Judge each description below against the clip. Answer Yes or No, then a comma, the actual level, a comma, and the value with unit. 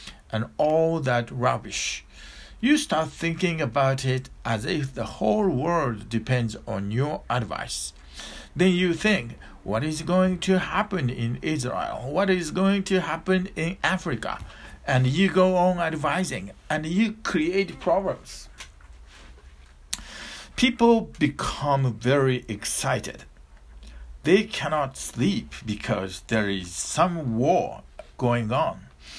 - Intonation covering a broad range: Yes, wide, 8.9 semitones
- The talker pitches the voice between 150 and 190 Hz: No, low, 135 Hz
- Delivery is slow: Yes, slow, 120 wpm